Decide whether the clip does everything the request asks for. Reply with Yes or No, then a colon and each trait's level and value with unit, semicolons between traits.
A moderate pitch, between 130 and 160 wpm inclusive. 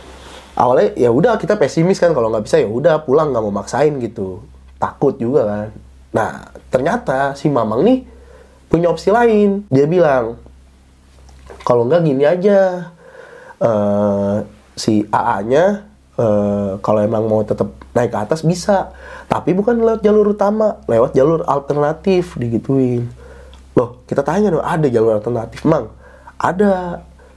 Yes: medium, 145 Hz; fast, 140 wpm